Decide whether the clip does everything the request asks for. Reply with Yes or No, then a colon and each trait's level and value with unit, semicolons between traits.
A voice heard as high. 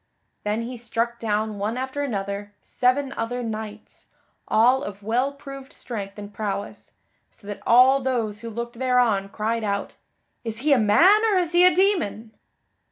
Yes: high, 230 Hz